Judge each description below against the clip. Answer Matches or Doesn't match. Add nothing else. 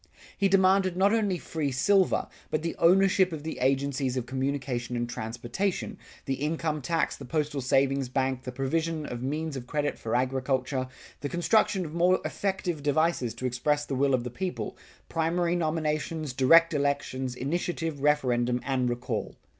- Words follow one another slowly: Doesn't match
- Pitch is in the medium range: Matches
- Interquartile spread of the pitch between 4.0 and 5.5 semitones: Matches